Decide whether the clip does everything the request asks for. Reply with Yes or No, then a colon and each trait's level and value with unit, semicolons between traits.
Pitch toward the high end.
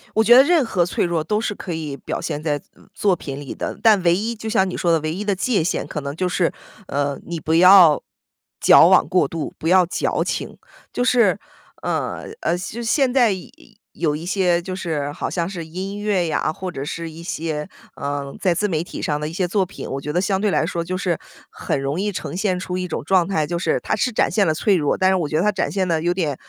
No: medium, 180 Hz